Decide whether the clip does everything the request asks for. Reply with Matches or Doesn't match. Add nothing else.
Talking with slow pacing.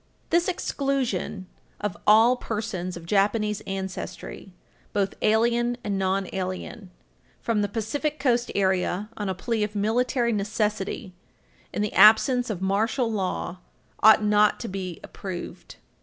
Matches